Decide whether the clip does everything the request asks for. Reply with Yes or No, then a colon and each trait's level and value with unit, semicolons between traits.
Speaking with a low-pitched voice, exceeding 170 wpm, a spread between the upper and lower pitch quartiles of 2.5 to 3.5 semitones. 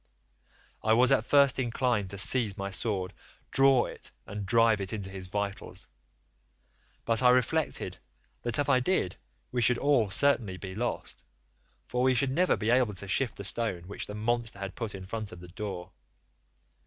No: low, 110 Hz; average, 180 wpm; average, 4.3 semitones